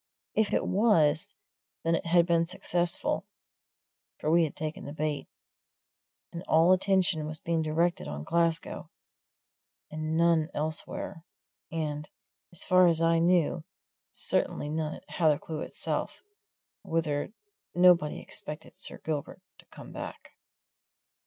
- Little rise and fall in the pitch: Yes, narrow, 2.0 semitones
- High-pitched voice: No, medium, 165 Hz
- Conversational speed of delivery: No, slow, 125 wpm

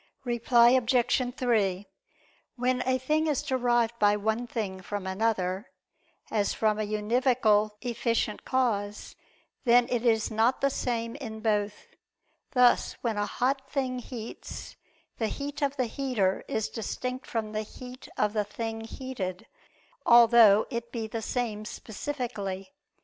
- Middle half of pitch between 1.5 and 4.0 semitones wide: Yes, average, 3.0 semitones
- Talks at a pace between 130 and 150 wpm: Yes, average, 140 wpm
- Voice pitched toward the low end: No, high, 230 Hz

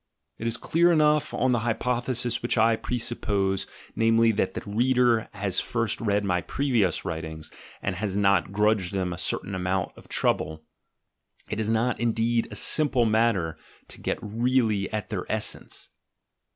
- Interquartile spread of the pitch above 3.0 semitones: Yes, average, 3.5 semitones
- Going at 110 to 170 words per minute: Yes, average, 155 wpm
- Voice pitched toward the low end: Yes, low, 110 Hz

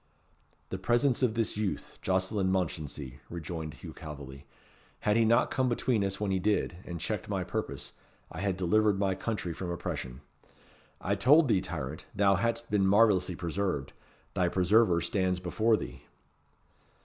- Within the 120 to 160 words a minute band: Yes, average, 155 wpm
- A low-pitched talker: Yes, very low, 95 Hz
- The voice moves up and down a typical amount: Yes, average, 3.9 semitones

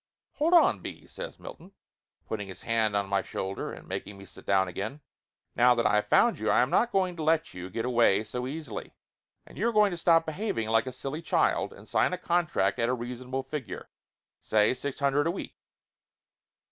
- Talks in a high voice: No, low, 125 Hz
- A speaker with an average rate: No, fast, 210 wpm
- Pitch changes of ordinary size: No, wide, 7.5 semitones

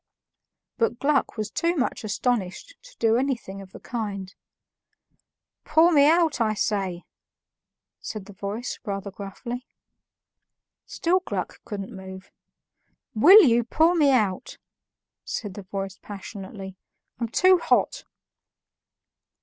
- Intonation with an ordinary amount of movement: No, wide, 6.1 semitones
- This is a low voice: No, high, 220 Hz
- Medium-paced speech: No, slow, 115 wpm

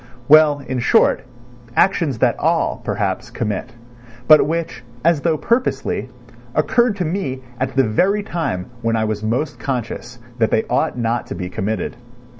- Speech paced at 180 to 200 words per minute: No, average, 155 wpm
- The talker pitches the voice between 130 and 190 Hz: Yes, low, 135 Hz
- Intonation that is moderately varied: No, wide, 6.5 semitones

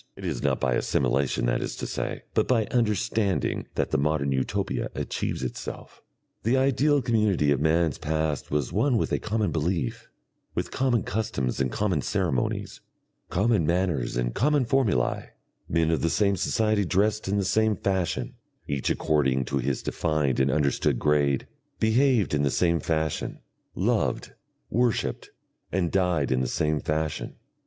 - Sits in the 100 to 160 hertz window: No, very low, 85 Hz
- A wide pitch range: Yes, wide, 7.2 semitones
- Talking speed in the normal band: Yes, average, 155 wpm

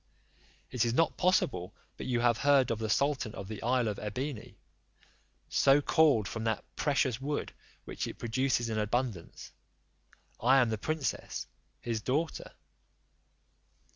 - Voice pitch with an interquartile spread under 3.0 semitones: No, average, 3.9 semitones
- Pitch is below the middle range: Yes, low, 120 Hz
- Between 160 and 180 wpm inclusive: No, average, 140 wpm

